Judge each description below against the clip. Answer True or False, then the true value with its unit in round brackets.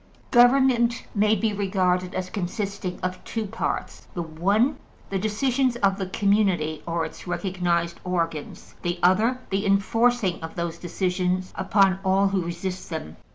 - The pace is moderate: True (145 wpm)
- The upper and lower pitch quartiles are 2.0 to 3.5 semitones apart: True (3.2 semitones)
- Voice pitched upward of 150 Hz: True (190 Hz)